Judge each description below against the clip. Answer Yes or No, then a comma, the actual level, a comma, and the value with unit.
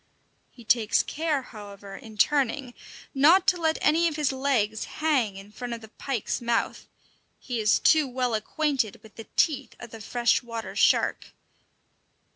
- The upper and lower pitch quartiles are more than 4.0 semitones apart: Yes, average, 5.1 semitones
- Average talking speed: Yes, average, 160 wpm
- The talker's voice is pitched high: Yes, high, 245 Hz